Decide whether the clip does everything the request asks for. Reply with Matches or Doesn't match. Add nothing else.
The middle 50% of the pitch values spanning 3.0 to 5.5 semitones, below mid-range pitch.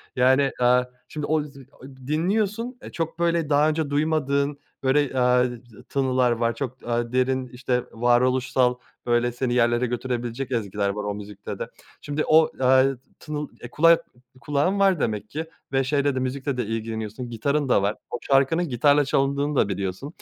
Matches